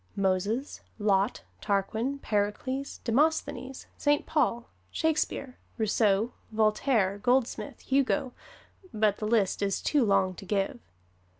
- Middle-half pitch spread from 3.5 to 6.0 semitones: Yes, average, 4.8 semitones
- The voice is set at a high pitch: Yes, high, 225 Hz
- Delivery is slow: Yes, slow, 105 wpm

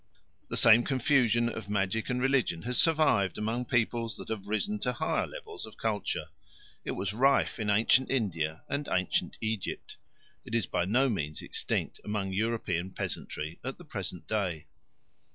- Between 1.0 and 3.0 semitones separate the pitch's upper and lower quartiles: No, average, 4.4 semitones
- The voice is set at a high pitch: No, low, 110 Hz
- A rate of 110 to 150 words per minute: No, average, 160 wpm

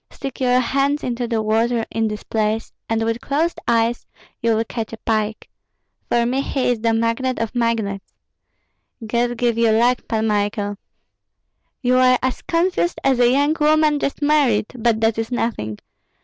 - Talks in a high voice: Yes, high, 235 Hz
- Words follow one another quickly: No, average, 170 wpm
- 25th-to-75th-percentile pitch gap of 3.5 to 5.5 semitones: No, narrow, 2.4 semitones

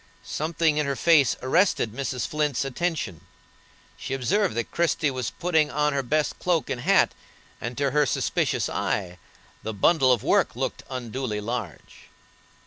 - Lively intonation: No, average, 4.5 semitones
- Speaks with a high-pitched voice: No, medium, 140 Hz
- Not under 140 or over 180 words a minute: Yes, average, 150 wpm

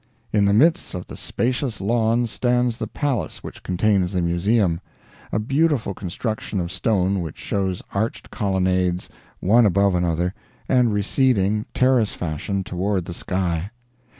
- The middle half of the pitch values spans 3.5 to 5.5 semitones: Yes, average, 4.1 semitones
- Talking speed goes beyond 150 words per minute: No, average, 140 wpm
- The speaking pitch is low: Yes, low, 100 Hz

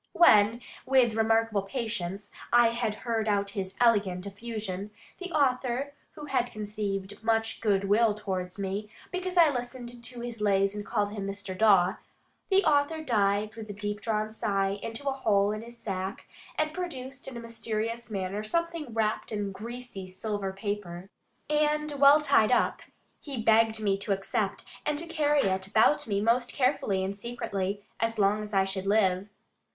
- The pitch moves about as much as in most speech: Yes, average, 3.5 semitones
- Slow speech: No, average, 165 wpm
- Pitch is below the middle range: No, high, 220 Hz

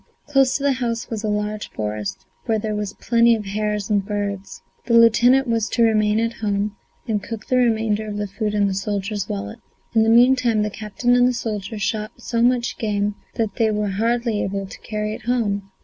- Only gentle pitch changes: Yes, narrow, 2.1 semitones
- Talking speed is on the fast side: Yes, fast, 210 wpm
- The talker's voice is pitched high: Yes, high, 215 Hz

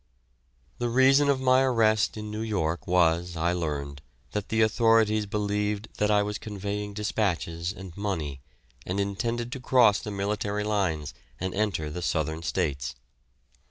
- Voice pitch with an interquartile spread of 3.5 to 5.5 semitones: Yes, average, 3.9 semitones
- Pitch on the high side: No, low, 105 Hz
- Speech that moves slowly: No, average, 150 wpm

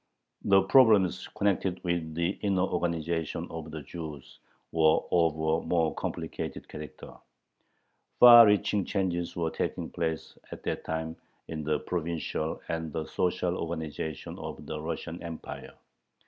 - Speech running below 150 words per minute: Yes, slow, 135 wpm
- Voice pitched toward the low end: Yes, very low, 85 Hz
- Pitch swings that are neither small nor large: No, narrow, 2.2 semitones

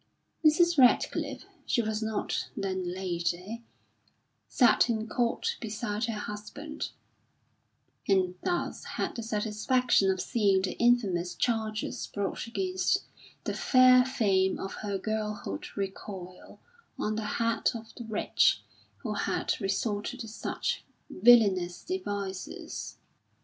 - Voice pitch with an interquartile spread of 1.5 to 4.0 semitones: Yes, average, 3.6 semitones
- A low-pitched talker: No, high, 215 Hz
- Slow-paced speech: Yes, slow, 115 wpm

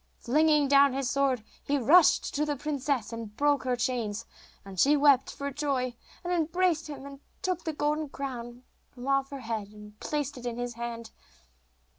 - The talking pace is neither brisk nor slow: Yes, average, 180 wpm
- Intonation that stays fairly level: No, average, 3.5 semitones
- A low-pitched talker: No, very high, 275 Hz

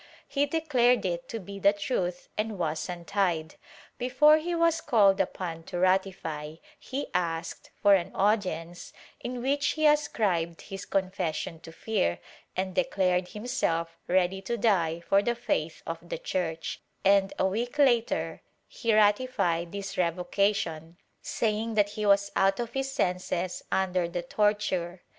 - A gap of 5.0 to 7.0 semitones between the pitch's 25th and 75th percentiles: No, average, 4.5 semitones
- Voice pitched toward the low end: No, high, 195 Hz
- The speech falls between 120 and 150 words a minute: Yes, average, 145 wpm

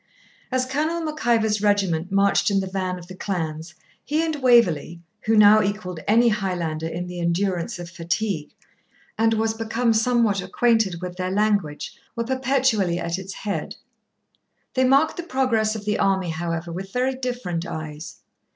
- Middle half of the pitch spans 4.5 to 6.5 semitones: Yes, average, 4.9 semitones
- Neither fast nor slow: Yes, average, 160 wpm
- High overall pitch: Yes, high, 200 Hz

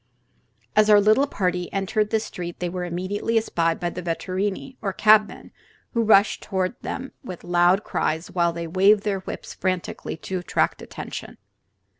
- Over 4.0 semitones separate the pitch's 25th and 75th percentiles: No, average, 3.2 semitones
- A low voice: No, high, 190 Hz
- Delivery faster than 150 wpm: Yes, average, 160 wpm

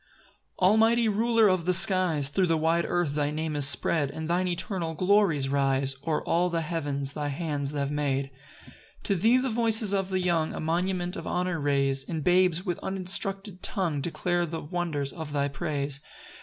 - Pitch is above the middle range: No, medium, 170 Hz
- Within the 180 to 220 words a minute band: Yes, average, 185 wpm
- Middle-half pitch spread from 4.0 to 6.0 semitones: Yes, average, 4.3 semitones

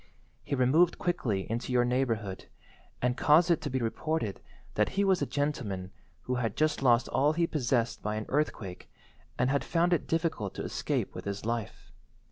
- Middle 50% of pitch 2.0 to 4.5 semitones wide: No, wide, 5.5 semitones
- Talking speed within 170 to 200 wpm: Yes, average, 180 wpm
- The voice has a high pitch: No, low, 125 Hz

